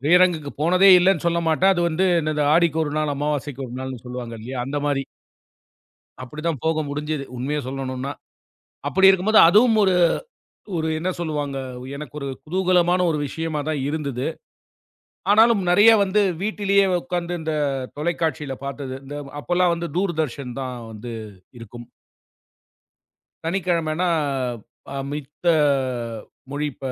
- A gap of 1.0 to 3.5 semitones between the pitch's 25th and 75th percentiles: No, average, 4.2 semitones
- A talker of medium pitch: Yes, medium, 155 Hz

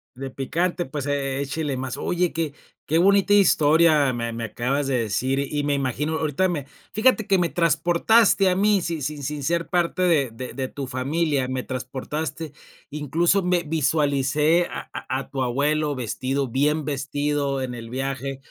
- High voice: No, medium, 145 Hz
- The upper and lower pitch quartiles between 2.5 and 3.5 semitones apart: No, average, 3.9 semitones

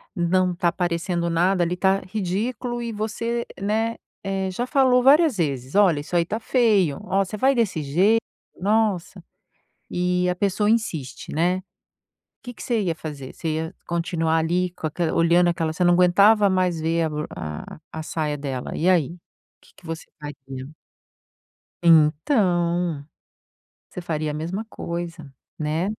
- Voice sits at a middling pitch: Yes, medium, 175 Hz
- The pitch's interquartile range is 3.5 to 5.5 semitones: Yes, average, 4.1 semitones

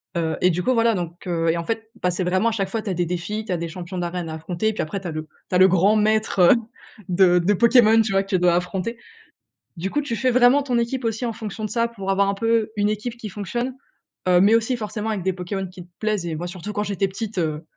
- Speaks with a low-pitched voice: No, high, 195 Hz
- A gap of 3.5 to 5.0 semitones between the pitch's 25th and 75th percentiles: Yes, average, 4.0 semitones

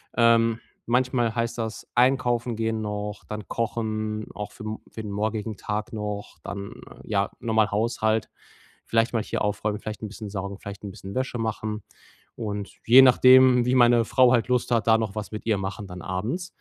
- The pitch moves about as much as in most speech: No, narrow, 2.1 semitones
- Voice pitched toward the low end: Yes, low, 110 Hz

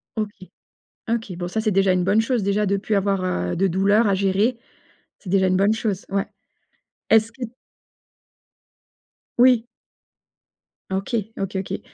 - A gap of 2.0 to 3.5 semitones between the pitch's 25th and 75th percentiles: Yes, narrow, 2.6 semitones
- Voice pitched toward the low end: No, high, 200 Hz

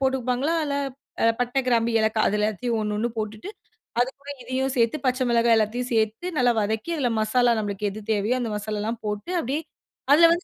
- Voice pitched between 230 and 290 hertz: Yes, high, 235 Hz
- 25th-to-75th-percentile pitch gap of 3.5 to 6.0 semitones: No, average, 3.0 semitones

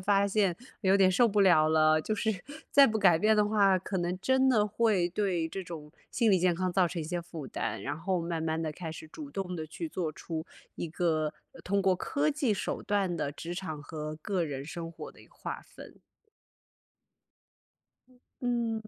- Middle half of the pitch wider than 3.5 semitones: Yes, average, 4.2 semitones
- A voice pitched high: No, medium, 180 Hz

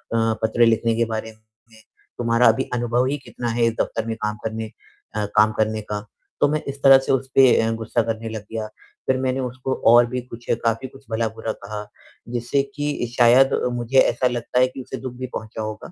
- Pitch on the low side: Yes, low, 115 Hz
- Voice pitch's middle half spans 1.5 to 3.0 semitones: Yes, narrow, 2.4 semitones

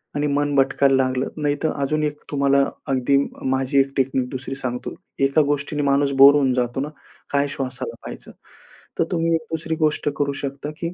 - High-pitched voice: No, medium, 140 Hz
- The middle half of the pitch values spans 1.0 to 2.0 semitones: Yes, narrow, 1.7 semitones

